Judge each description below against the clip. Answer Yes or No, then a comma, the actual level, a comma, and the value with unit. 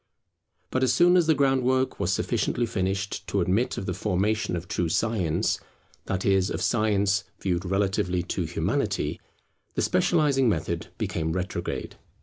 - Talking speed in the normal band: Yes, average, 145 wpm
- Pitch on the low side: Yes, low, 100 Hz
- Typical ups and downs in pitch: No, wide, 5.8 semitones